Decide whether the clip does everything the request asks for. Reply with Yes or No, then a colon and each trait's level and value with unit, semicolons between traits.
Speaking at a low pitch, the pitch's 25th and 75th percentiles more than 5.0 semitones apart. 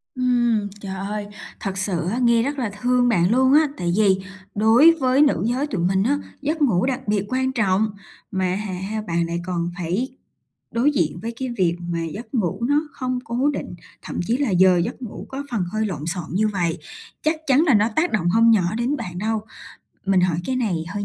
No: high, 215 Hz; wide, 5.4 semitones